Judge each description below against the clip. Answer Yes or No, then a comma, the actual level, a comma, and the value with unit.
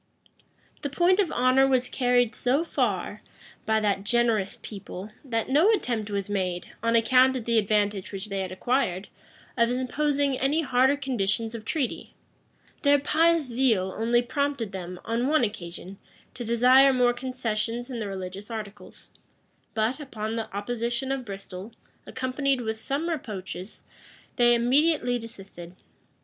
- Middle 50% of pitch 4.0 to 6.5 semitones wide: Yes, average, 4.3 semitones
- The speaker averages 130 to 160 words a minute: Yes, average, 145 wpm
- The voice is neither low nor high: No, high, 235 Hz